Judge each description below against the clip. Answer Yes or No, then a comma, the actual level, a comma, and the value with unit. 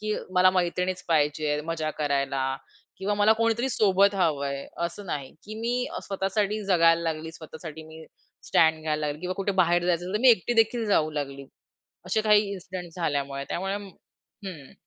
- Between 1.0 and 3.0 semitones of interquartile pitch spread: No, average, 4.6 semitones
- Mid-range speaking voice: Yes, medium, 175 Hz